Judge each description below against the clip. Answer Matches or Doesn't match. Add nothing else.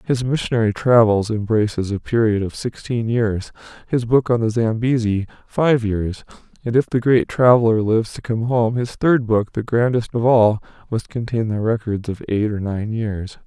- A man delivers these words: Matches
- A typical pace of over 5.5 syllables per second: Doesn't match